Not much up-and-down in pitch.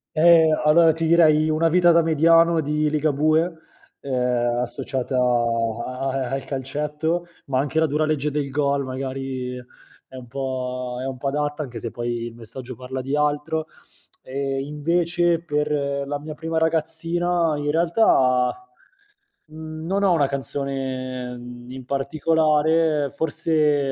No: average, 3.6 semitones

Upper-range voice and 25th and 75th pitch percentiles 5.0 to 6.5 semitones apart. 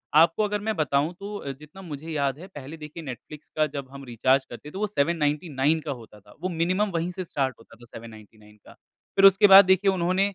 No: medium, 155 Hz; wide, 5.5 semitones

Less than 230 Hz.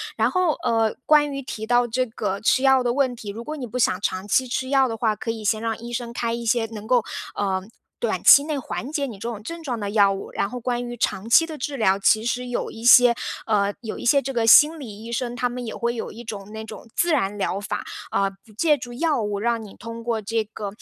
No: high, 235 Hz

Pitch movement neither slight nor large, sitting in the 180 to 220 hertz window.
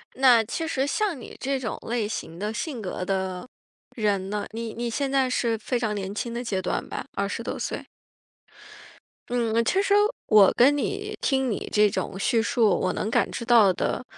No: average, 3.9 semitones; high, 230 Hz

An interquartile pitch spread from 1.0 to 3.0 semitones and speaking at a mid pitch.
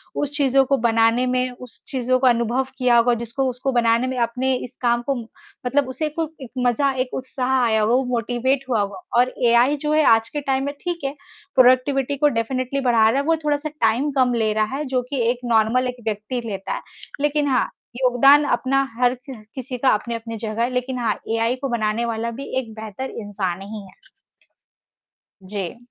No: narrow, 2.6 semitones; very high, 250 Hz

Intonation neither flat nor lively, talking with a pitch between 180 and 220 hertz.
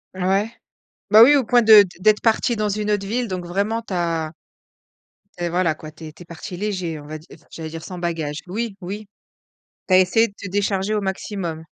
Yes: average, 3.9 semitones; high, 190 Hz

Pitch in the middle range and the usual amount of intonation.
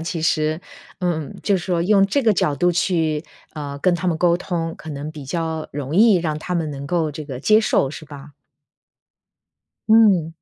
Yes: medium, 165 Hz; average, 3.0 semitones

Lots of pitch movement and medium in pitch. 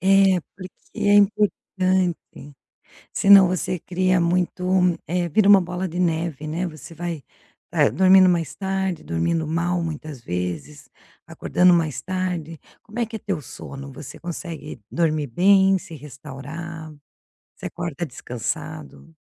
No: average, 3.2 semitones; medium, 175 Hz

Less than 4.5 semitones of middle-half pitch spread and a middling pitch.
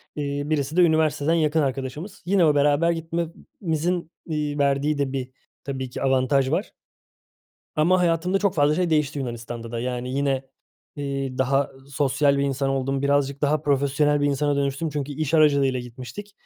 Yes: narrow, 2.5 semitones; medium, 145 Hz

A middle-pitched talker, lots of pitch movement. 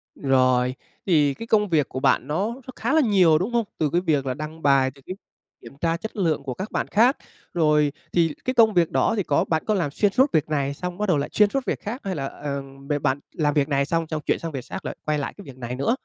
Yes: medium, 155 Hz; wide, 6.2 semitones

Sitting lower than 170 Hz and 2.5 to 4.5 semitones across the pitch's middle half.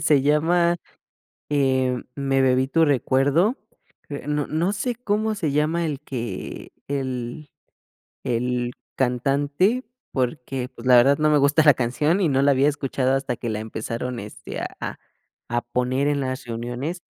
Yes: low, 135 Hz; average, 3.3 semitones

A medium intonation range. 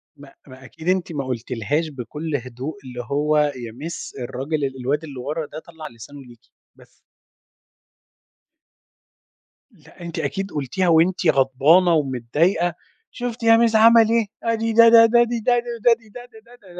No: wide, 8.6 semitones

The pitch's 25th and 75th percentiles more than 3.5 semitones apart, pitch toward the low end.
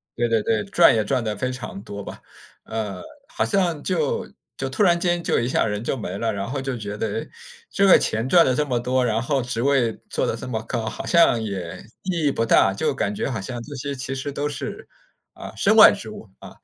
Yes: average, 4.4 semitones; low, 125 Hz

